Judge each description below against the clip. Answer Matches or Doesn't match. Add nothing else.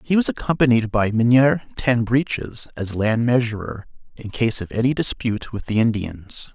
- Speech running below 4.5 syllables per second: Doesn't match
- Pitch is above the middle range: Doesn't match